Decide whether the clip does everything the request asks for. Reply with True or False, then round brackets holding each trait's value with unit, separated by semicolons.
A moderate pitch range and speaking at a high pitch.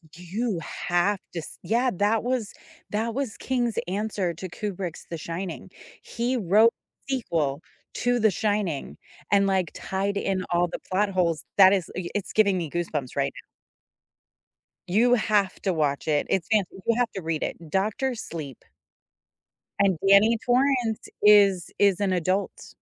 True (4.0 semitones; 195 Hz)